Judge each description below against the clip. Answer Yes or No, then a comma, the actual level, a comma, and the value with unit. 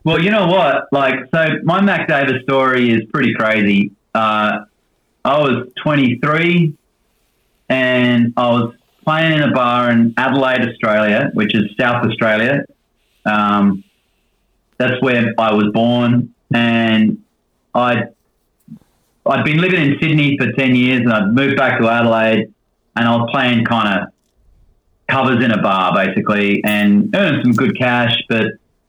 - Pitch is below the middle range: Yes, low, 120 Hz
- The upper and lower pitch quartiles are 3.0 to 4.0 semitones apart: Yes, average, 3.6 semitones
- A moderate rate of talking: Yes, average, 145 wpm